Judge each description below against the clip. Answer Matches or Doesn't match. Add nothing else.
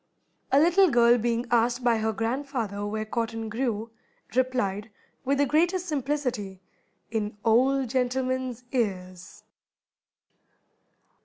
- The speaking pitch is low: Doesn't match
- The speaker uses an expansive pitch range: Doesn't match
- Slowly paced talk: Matches